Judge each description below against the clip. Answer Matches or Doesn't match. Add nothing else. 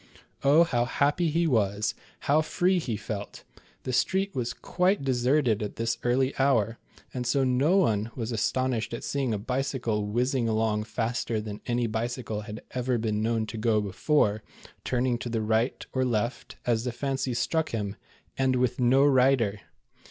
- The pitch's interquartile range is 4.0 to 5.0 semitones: Doesn't match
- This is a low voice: Matches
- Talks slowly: Doesn't match